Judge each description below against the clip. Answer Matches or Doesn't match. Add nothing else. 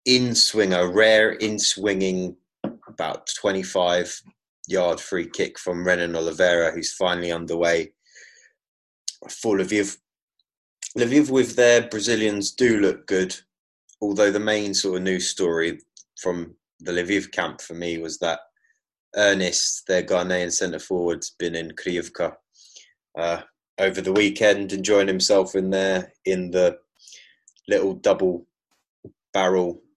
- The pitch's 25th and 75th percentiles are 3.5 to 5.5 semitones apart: Doesn't match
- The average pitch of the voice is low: Matches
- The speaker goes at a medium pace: Doesn't match